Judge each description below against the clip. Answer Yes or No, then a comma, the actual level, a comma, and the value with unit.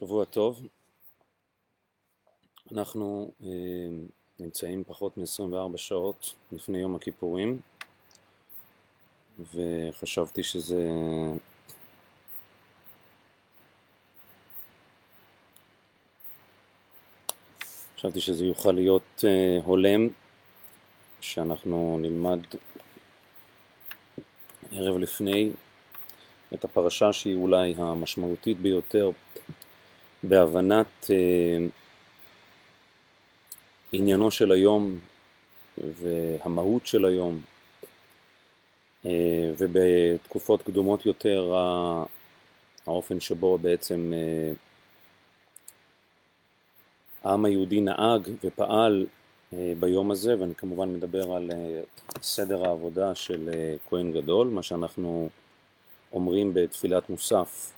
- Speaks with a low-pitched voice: Yes, very low, 90 Hz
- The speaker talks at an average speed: No, slow, 70 wpm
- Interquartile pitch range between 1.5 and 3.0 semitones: Yes, narrow, 2.4 semitones